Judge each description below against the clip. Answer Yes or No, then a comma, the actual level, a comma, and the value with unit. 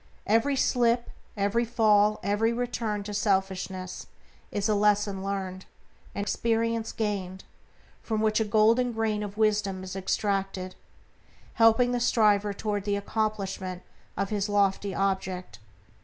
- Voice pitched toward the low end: No, high, 205 Hz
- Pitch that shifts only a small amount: Yes, narrow, 2.3 semitones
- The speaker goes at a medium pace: No, slow, 125 wpm